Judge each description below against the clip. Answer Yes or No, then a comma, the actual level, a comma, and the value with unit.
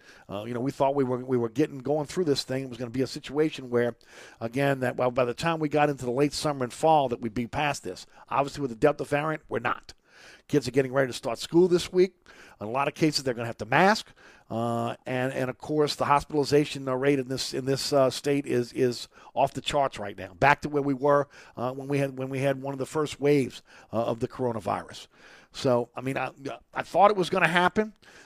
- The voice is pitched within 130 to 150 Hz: Yes, low, 135 Hz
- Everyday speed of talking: No, fast, 260 wpm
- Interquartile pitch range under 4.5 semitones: Yes, average, 2.8 semitones